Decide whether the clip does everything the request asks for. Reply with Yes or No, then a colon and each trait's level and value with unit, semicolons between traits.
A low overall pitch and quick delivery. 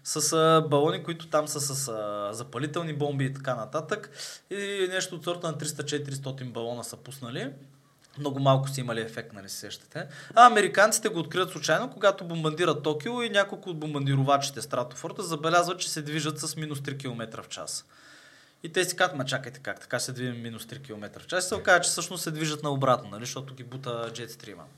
No: medium, 150 Hz; fast, 190 wpm